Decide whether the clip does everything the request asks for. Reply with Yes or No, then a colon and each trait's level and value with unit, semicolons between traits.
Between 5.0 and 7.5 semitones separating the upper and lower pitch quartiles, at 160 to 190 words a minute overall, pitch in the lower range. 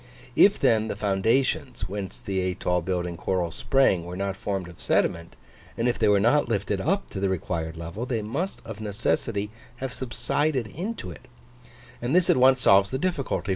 Yes: wide, 5.4 semitones; average, 180 wpm; low, 105 Hz